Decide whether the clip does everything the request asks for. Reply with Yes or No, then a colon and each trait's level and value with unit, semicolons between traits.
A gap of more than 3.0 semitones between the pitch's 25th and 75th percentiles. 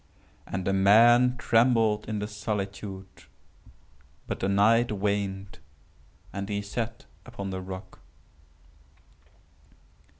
No: narrow, 2.6 semitones